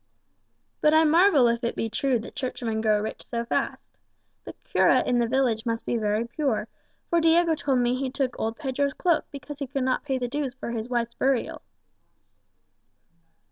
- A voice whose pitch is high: Yes, very high, 255 Hz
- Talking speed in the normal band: Yes, average, 185 wpm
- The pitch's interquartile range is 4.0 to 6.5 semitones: No, average, 3.4 semitones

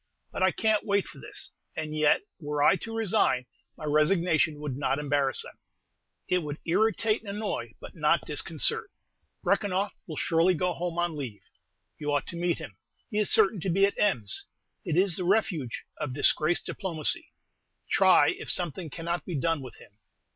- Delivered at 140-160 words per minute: No, average, 175 wpm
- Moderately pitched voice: Yes, medium, 170 Hz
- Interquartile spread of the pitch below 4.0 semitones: No, average, 4.6 semitones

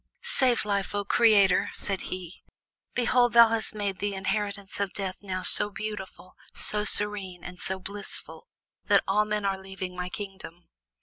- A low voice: No, high, 200 Hz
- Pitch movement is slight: Yes, narrow, 1.8 semitones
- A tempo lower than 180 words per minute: Yes, average, 160 wpm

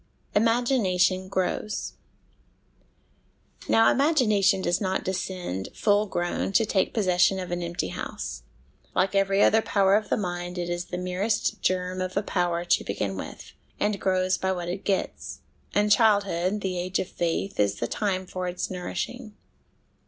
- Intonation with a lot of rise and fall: No, narrow, 2.5 semitones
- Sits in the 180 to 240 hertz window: Yes, medium, 185 Hz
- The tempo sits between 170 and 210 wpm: No, average, 155 wpm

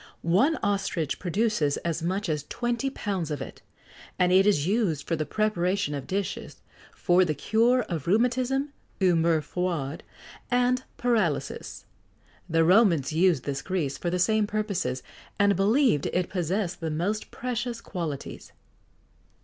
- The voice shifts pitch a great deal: No, average, 5.0 semitones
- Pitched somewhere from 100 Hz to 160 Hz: No, medium, 185 Hz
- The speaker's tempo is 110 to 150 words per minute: Yes, average, 140 wpm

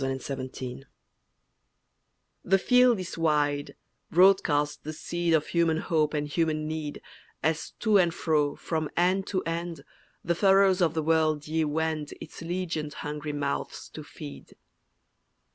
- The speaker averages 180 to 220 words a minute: No, average, 140 wpm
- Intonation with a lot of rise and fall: No, average, 2.7 semitones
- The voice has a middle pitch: Yes, medium, 160 Hz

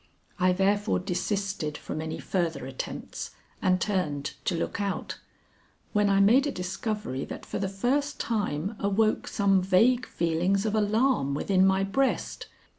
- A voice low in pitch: No, high, 195 Hz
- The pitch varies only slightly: No, average, 3.2 semitones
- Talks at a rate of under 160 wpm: Yes, average, 145 wpm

